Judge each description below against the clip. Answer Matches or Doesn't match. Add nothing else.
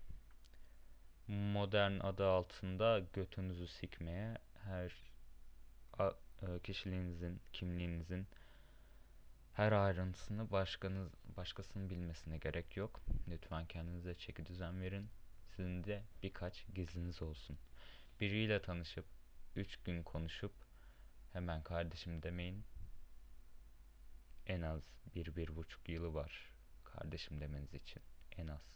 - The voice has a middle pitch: Doesn't match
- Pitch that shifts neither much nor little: Matches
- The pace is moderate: Doesn't match